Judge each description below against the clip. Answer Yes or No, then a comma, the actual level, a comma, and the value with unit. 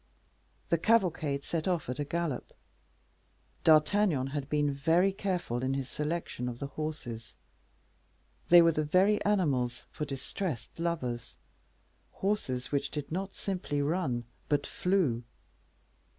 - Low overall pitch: No, medium, 150 Hz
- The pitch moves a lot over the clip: No, average, 4.8 semitones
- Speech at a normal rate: No, slow, 125 wpm